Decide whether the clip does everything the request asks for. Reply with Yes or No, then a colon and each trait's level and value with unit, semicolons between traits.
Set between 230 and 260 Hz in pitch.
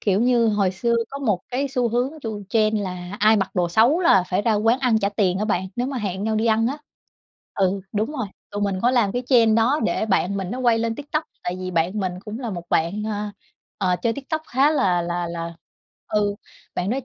No: high, 215 Hz